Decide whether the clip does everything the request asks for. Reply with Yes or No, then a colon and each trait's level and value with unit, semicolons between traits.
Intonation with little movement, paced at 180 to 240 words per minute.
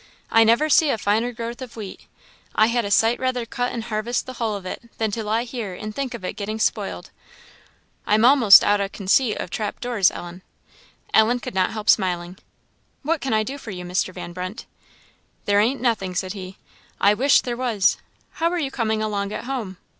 No: average, 3.5 semitones; fast, 205 wpm